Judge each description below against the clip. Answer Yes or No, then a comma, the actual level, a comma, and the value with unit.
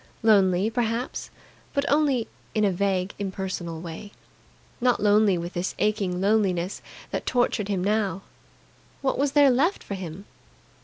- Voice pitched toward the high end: Yes, high, 205 Hz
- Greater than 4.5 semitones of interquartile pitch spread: No, average, 3.8 semitones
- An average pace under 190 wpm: Yes, average, 140 wpm